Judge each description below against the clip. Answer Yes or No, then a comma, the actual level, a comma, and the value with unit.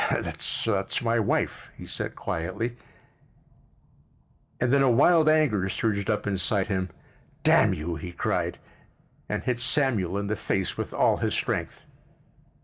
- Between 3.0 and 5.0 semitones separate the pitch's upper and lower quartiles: Yes, average, 4.4 semitones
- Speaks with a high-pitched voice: No, low, 105 Hz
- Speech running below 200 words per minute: Yes, slow, 135 wpm